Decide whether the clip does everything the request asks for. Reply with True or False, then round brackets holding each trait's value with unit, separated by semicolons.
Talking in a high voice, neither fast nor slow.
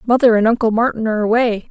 False (225 Hz; 210 wpm)